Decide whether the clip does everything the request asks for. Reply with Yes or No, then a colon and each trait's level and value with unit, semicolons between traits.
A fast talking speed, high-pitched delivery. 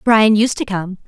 Yes: fast, 225 wpm; high, 210 Hz